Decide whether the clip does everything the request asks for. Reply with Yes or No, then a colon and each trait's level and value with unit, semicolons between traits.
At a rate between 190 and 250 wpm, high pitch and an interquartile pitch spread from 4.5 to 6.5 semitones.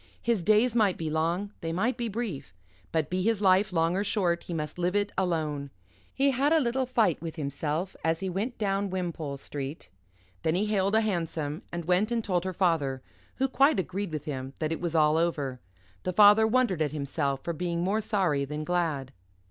No: fast, 205 wpm; medium, 175 Hz; average, 5.0 semitones